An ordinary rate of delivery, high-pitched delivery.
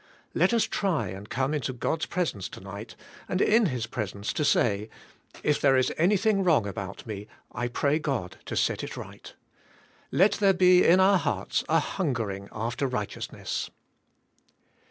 No: average, 160 wpm; low, 135 Hz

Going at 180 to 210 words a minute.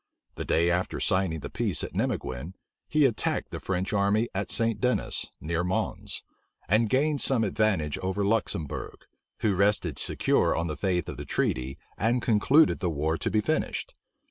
No: average, 170 wpm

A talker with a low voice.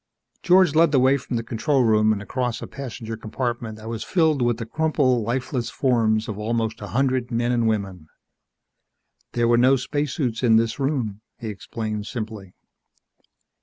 Yes: low, 120 Hz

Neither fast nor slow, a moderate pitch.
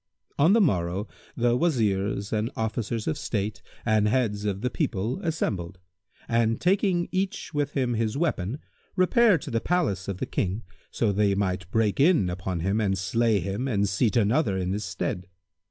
No: average, 170 wpm; low, 110 Hz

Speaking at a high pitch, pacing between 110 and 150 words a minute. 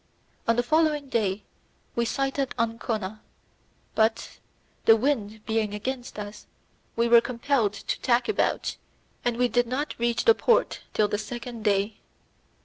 Yes: high, 230 Hz; average, 140 wpm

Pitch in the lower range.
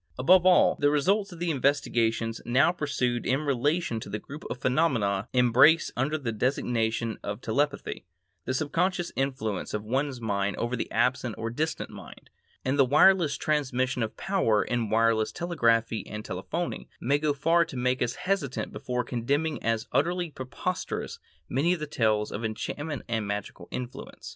Yes: low, 130 Hz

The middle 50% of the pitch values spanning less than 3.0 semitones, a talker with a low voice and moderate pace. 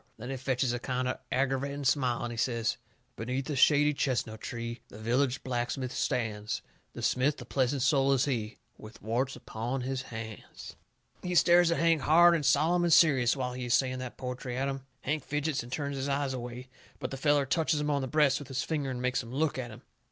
No: narrow, 2.6 semitones; low, 130 Hz; fast, 220 wpm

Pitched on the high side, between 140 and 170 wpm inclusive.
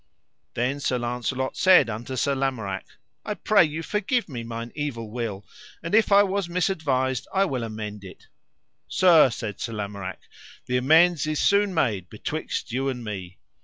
No: low, 130 Hz; average, 165 wpm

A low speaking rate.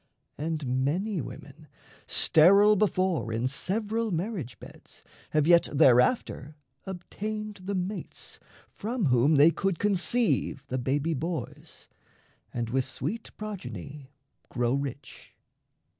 Yes: slow, 110 wpm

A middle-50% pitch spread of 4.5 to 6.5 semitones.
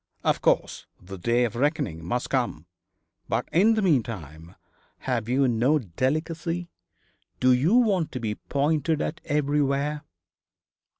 Yes: average, 5.1 semitones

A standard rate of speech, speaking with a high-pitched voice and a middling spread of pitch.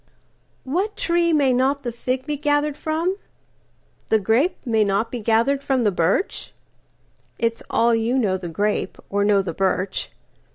No: average, 150 wpm; high, 235 Hz; wide, 5.7 semitones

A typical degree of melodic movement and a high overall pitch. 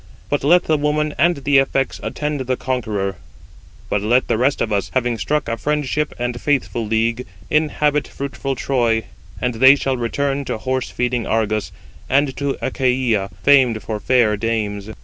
No: average, 3.9 semitones; low, 130 Hz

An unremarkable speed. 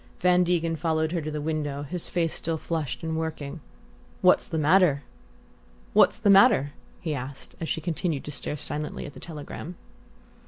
Yes: average, 155 wpm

